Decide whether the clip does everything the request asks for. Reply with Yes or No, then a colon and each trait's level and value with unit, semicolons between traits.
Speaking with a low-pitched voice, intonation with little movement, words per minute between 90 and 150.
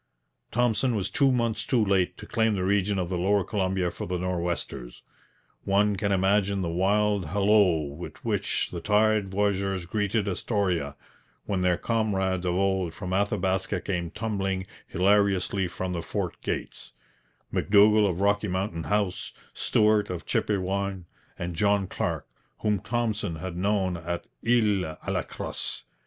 Yes: very low, 95 Hz; narrow, 2.3 semitones; average, 145 wpm